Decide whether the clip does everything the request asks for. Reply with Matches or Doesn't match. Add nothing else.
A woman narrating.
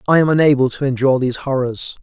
Doesn't match